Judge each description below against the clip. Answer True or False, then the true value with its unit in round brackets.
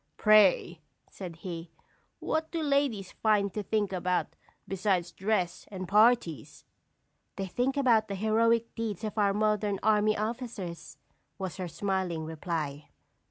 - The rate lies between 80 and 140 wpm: True (135 wpm)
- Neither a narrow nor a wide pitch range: True (3.3 semitones)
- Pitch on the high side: True (205 Hz)